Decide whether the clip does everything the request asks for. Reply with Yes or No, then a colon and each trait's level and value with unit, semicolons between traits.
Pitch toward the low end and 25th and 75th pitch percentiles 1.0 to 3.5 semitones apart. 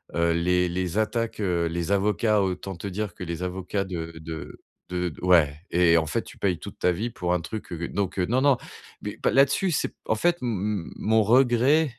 No: very low, 95 Hz; average, 4.2 semitones